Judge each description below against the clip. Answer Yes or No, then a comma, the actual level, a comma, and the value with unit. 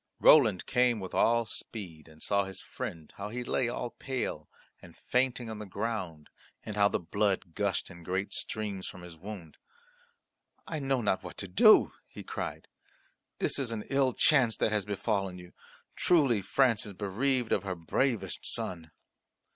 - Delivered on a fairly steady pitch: No, average, 4.5 semitones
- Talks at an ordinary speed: Yes, average, 170 wpm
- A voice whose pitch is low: Yes, low, 105 Hz